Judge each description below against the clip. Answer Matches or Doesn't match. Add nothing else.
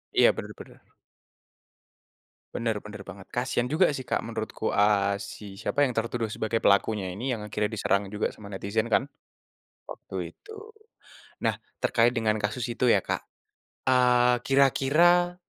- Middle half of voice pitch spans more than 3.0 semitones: Matches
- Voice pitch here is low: Matches